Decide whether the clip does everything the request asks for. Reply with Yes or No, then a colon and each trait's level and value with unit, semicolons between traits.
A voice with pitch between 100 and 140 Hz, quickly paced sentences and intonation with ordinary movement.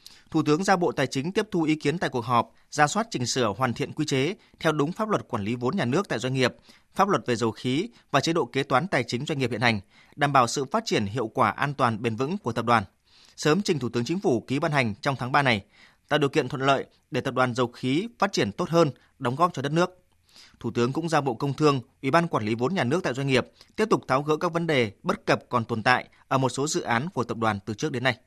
Yes: low, 135 Hz; fast, 290 wpm; average, 4.6 semitones